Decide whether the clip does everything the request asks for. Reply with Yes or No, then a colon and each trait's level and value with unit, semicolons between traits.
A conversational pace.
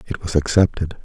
Yes: average, 175 wpm